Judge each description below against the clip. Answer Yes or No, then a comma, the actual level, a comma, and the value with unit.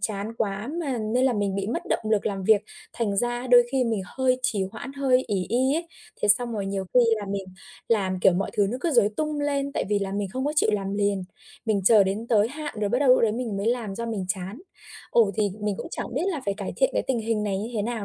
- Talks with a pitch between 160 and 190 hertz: No, high, 220 Hz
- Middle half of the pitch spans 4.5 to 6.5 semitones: No, average, 3.9 semitones